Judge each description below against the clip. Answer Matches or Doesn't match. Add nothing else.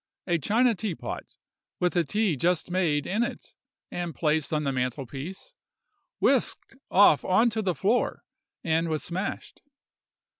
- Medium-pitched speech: Matches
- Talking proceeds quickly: Doesn't match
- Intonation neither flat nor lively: Matches